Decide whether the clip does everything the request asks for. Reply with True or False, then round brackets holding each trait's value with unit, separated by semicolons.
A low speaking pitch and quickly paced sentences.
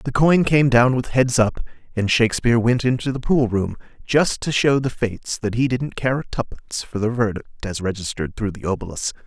True (120 Hz; 215 wpm)